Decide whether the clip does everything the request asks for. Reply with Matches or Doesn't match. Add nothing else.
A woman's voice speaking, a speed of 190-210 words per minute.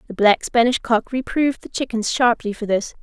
Matches